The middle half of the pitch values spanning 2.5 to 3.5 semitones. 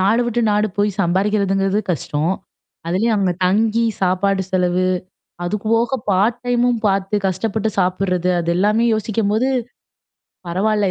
Yes: average, 2.9 semitones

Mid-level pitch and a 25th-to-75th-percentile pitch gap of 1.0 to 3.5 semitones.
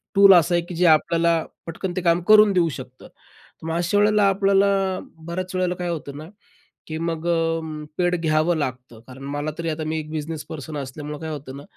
Yes: medium, 165 Hz; narrow, 2.6 semitones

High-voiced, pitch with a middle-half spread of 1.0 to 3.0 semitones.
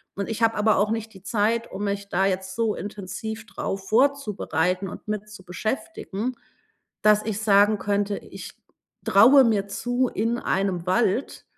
Yes: high, 210 Hz; narrow, 2.4 semitones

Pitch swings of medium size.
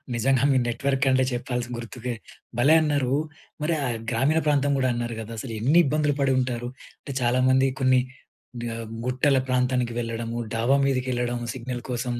No: narrow, 2.1 semitones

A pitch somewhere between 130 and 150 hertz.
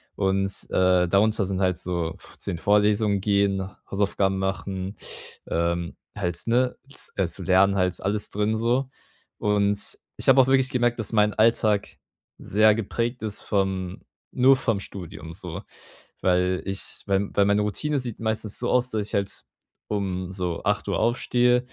No: low, 100 Hz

